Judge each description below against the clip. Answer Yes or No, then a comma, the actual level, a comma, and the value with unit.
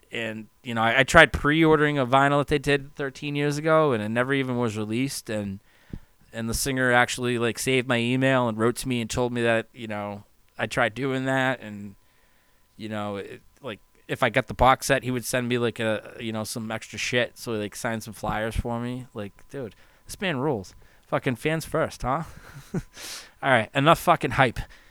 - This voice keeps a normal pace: No, fast, 215 wpm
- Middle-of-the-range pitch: No, low, 120 Hz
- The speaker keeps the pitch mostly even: No, average, 3.5 semitones